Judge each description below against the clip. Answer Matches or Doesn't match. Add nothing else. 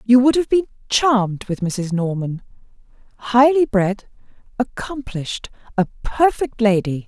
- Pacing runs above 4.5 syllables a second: Doesn't match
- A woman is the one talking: Matches